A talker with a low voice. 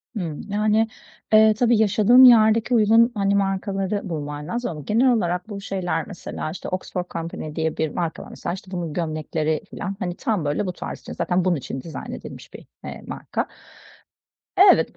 No: medium, 185 Hz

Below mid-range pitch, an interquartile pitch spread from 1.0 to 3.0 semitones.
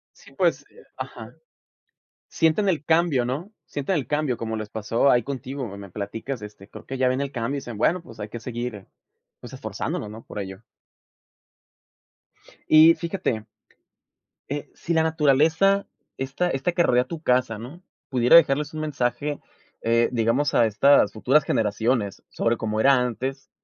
No: low, 130 Hz; average, 5.0 semitones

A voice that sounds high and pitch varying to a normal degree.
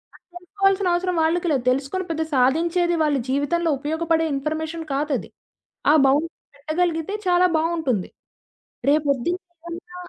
Yes: very high, 325 Hz; average, 3.2 semitones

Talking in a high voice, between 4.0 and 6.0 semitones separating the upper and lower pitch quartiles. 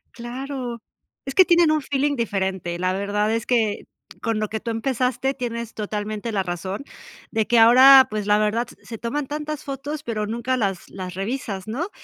Yes: high, 230 Hz; average, 4.3 semitones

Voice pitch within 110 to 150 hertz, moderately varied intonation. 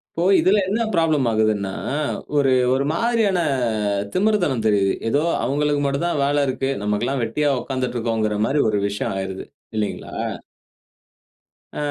No: low, 135 Hz; wide, 5.9 semitones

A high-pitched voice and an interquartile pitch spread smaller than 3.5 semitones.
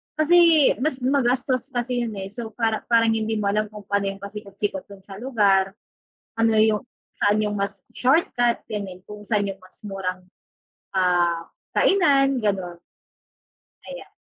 No: high, 215 Hz; average, 3.8 semitones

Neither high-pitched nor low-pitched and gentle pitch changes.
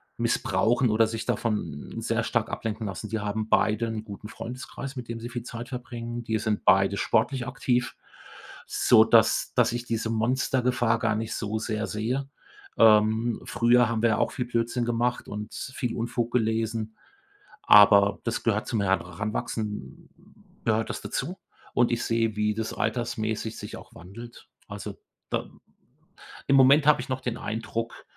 No: low, 115 Hz; narrow, 1.9 semitones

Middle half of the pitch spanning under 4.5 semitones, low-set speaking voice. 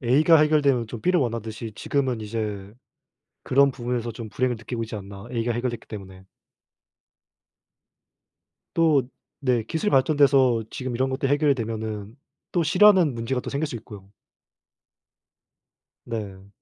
Yes: average, 4.0 semitones; low, 120 Hz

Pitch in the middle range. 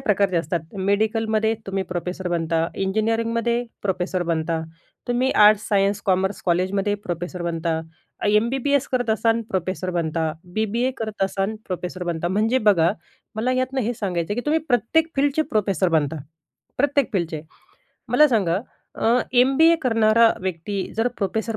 No: high, 205 Hz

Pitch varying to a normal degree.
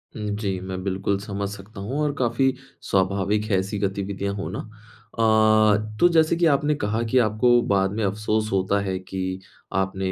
No: narrow, 2.2 semitones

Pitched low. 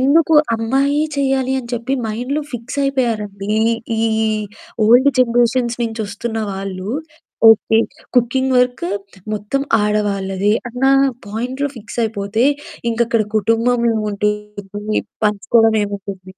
No: high, 225 Hz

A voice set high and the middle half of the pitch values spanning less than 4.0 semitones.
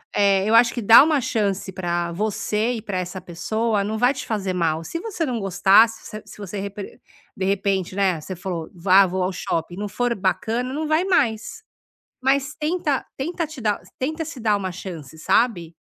No: high, 205 Hz; average, 4.8 semitones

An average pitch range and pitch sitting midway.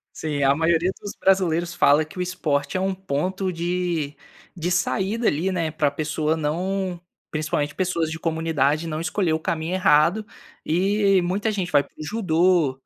Yes: average, 3.2 semitones; medium, 170 Hz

